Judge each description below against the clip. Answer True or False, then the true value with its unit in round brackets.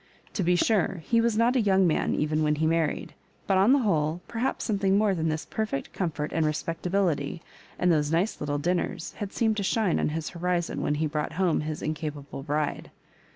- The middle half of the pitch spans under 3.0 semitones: False (4.5 semitones)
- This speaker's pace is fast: True (210 wpm)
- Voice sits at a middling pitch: True (170 Hz)